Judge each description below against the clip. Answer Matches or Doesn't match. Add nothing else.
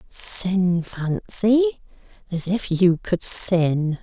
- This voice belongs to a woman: Matches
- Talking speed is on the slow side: Matches